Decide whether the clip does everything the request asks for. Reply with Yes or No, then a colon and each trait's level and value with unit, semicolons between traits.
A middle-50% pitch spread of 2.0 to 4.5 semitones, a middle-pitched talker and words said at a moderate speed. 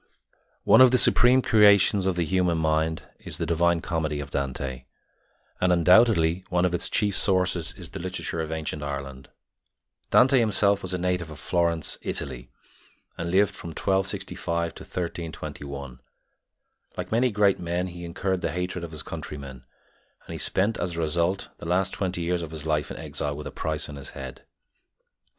No: average, 3.2 semitones; very low, 85 Hz; average, 175 wpm